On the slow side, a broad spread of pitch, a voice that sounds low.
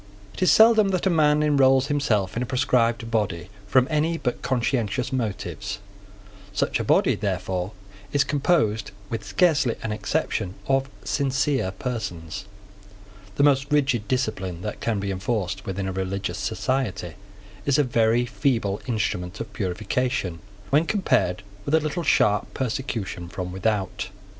No: average, 145 wpm; wide, 5.8 semitones; low, 115 Hz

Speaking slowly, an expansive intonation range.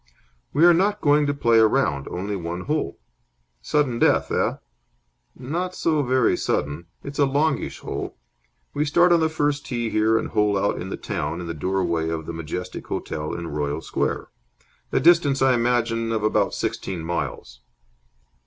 No: average, 170 wpm; wide, 8.9 semitones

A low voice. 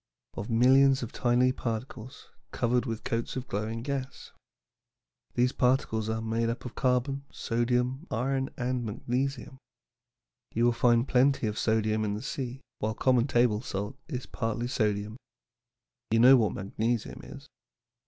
Yes: low, 120 Hz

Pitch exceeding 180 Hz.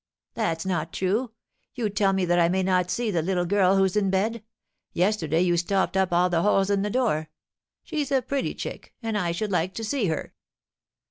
Yes: high, 190 Hz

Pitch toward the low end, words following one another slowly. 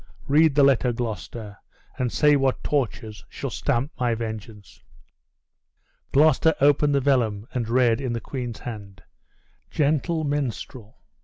Yes: low, 125 Hz; slow, 130 wpm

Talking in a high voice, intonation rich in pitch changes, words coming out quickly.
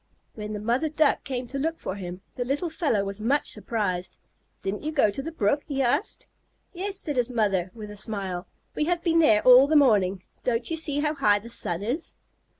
Yes: high, 245 Hz; wide, 6.5 semitones; fast, 215 wpm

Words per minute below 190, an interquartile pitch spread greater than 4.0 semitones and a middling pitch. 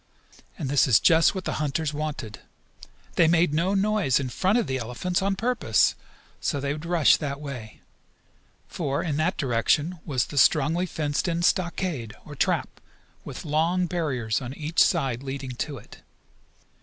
Yes: average, 165 wpm; average, 4.4 semitones; medium, 150 Hz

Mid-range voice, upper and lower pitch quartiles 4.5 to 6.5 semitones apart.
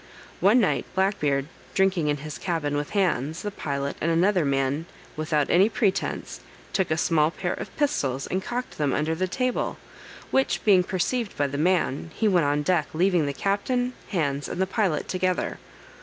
Yes: medium, 175 Hz; average, 5.0 semitones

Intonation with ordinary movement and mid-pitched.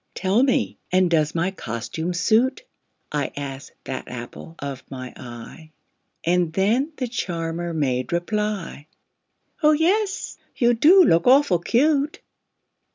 No: wide, 8.7 semitones; medium, 175 Hz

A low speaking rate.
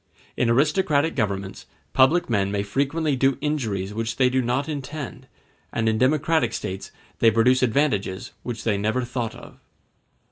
No: average, 150 wpm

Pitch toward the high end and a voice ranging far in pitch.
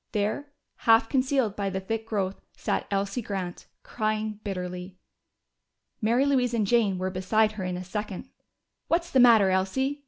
No: high, 215 Hz; average, 3.8 semitones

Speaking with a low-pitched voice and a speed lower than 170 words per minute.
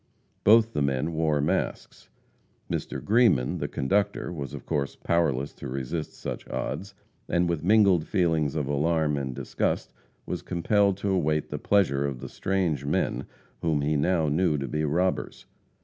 Yes: very low, 80 Hz; average, 160 wpm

